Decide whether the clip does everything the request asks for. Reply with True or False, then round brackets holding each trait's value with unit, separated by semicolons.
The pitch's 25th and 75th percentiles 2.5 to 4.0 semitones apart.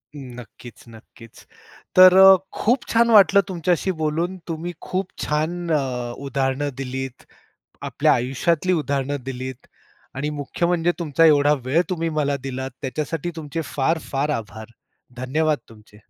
False (4.6 semitones)